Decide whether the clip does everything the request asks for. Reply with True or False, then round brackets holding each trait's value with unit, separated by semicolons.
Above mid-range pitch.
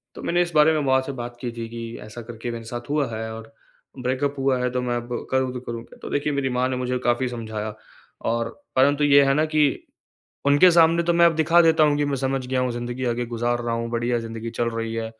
False (125 Hz)